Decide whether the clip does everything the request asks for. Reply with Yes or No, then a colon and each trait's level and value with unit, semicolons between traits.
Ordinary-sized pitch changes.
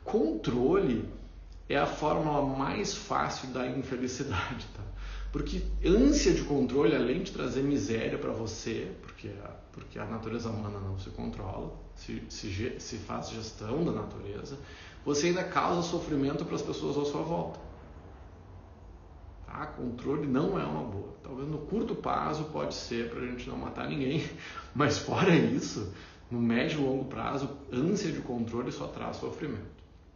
No: wide, 6.5 semitones